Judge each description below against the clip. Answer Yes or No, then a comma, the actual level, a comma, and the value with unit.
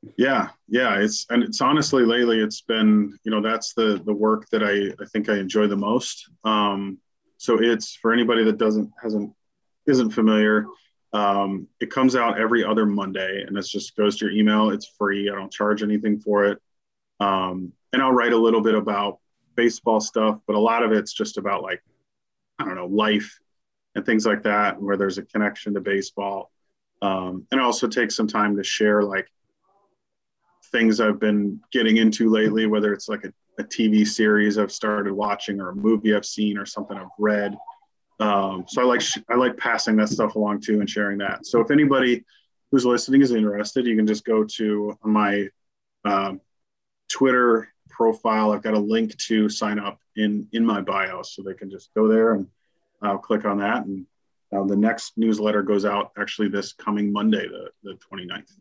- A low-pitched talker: Yes, low, 105 Hz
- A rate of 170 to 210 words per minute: Yes, average, 195 wpm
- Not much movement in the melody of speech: Yes, narrow, 1.7 semitones